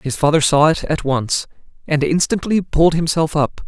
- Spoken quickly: No, average, 180 wpm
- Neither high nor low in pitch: Yes, medium, 155 Hz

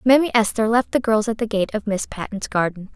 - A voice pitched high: Yes, high, 220 Hz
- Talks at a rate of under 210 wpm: No, fast, 245 wpm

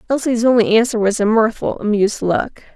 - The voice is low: No, high, 225 Hz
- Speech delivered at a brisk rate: No, average, 175 wpm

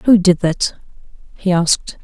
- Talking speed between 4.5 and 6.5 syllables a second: No, 4.2 syllables/s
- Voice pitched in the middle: Yes, medium, 180 Hz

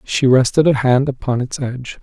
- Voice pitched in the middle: No, low, 130 Hz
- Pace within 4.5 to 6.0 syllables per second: Yes, 5.2 syllables/s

